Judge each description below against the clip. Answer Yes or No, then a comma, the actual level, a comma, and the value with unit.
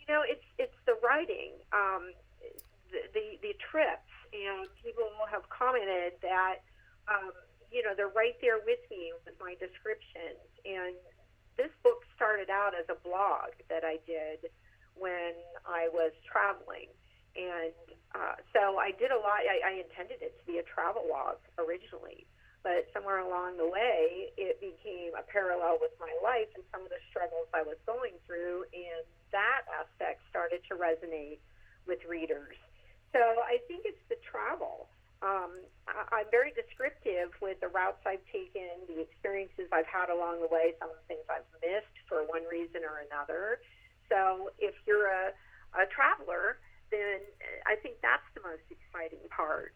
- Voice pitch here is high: Yes, high, 195 Hz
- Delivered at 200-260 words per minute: No, average, 165 wpm